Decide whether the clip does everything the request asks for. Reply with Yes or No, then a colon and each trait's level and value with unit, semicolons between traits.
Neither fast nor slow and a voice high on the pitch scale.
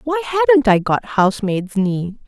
Yes: average, 160 wpm; high, 240 Hz